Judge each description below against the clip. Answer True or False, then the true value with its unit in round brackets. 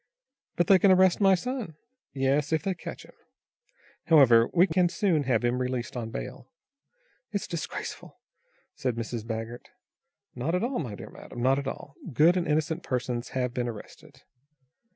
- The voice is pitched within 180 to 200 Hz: False (140 Hz)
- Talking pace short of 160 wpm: False (165 wpm)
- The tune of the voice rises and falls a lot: True (6.4 semitones)